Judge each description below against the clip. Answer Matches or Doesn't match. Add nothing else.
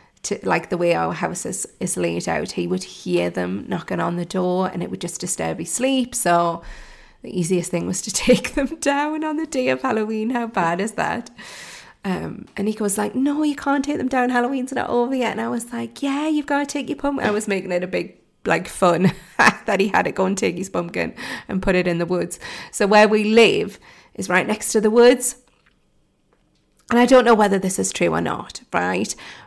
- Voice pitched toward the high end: Matches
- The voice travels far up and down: Matches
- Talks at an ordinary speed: Doesn't match